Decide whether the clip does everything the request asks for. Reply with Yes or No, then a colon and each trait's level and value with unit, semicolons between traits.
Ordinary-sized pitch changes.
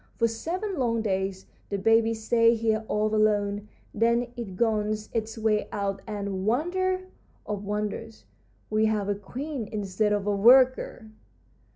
No: narrow, 2.1 semitones